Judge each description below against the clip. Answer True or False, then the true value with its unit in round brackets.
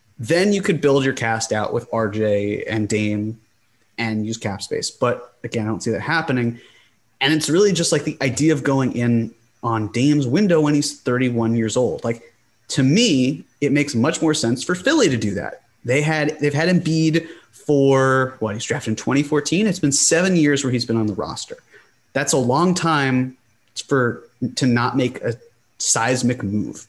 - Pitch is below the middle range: True (130 Hz)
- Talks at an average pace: True (190 wpm)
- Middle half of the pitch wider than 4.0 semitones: True (4.4 semitones)